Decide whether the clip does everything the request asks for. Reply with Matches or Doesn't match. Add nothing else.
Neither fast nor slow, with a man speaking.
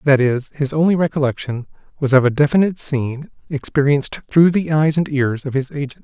Matches